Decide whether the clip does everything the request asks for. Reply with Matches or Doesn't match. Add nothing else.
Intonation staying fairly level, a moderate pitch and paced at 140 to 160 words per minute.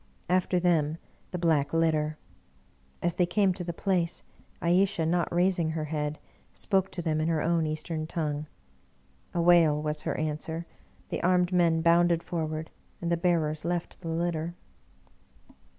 Matches